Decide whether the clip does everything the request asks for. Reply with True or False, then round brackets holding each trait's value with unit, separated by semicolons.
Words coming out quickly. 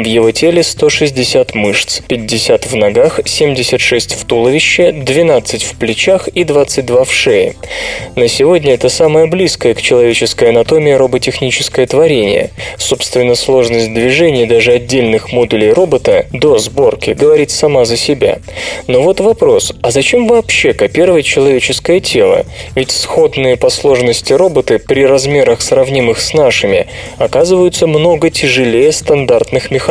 False (130 wpm)